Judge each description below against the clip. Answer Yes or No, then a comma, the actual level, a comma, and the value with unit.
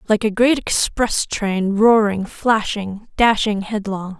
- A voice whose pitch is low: No, high, 210 Hz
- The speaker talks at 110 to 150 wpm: Yes, average, 145 wpm